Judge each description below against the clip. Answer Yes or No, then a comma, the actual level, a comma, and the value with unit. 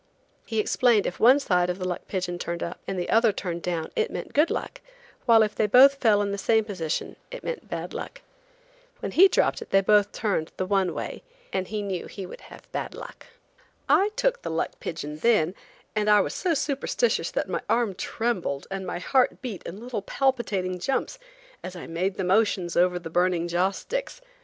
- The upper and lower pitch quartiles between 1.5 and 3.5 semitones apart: No, average, 5.0 semitones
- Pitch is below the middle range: No, high, 200 Hz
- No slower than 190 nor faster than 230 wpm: Yes, fast, 205 wpm